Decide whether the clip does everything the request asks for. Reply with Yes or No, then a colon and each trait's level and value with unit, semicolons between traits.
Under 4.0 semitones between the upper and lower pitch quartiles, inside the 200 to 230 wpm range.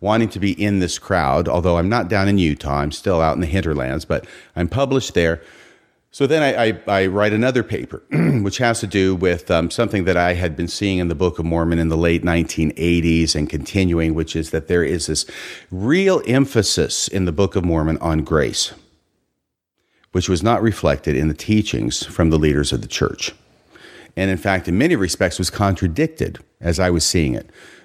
Yes: average, 3.4 semitones; fast, 205 wpm